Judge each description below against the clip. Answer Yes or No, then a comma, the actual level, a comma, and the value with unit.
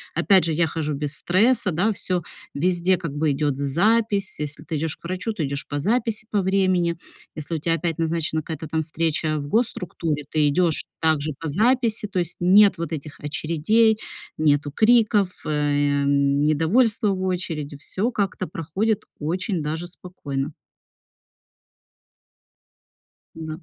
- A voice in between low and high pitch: Yes, medium, 165 Hz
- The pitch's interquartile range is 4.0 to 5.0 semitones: Yes, average, 4.4 semitones